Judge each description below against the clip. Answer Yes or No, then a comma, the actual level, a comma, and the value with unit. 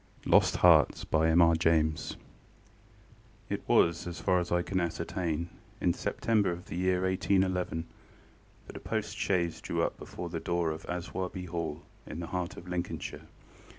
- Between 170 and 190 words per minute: No, average, 145 wpm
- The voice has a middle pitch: No, very low, 85 Hz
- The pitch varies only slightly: Yes, narrow, 1.7 semitones